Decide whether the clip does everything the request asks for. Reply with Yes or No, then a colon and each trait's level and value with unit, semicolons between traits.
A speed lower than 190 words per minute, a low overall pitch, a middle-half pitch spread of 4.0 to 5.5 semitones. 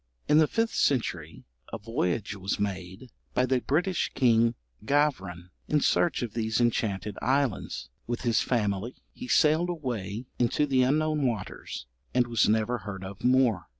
Yes: average, 150 wpm; low, 120 Hz; average, 5.2 semitones